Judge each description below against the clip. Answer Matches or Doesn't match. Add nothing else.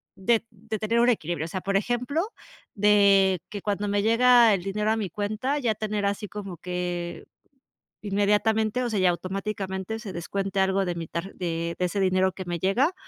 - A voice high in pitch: Matches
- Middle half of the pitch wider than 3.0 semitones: Doesn't match